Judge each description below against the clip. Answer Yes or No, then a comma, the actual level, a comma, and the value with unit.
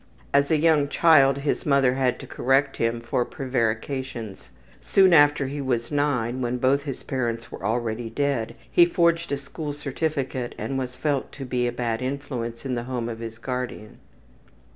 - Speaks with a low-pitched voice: Yes, low, 130 Hz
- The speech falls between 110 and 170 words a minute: No, average, 180 wpm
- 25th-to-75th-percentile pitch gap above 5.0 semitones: No, average, 3.2 semitones